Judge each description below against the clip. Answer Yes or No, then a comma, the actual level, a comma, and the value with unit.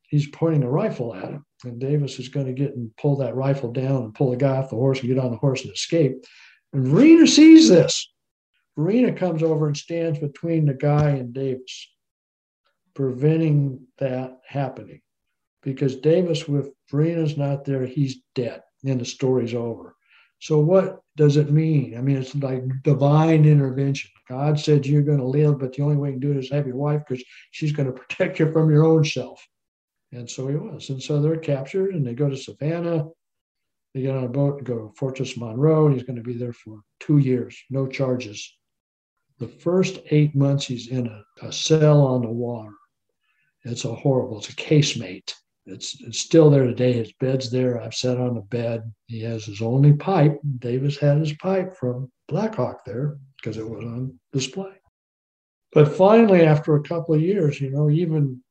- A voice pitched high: No, medium, 140 Hz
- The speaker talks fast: No, average, 195 wpm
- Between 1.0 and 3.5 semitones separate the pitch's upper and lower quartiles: Yes, average, 3.1 semitones